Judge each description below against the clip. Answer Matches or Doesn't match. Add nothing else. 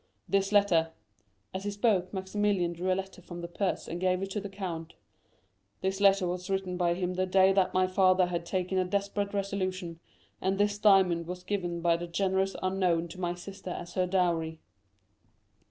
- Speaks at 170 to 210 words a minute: Matches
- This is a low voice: Doesn't match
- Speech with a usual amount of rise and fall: Doesn't match